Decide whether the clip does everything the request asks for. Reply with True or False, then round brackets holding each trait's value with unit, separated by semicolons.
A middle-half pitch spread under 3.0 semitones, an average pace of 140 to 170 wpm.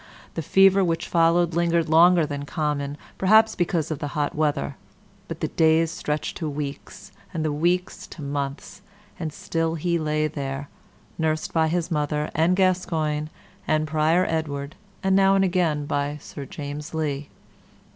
True (2.6 semitones; 155 wpm)